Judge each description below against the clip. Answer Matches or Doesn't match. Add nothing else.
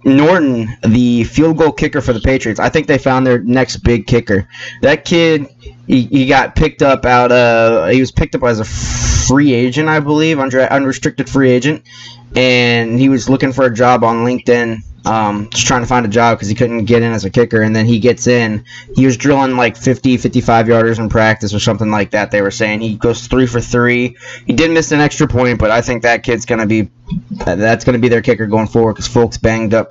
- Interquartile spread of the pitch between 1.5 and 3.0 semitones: Matches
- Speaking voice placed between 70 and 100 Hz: Doesn't match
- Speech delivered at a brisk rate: Matches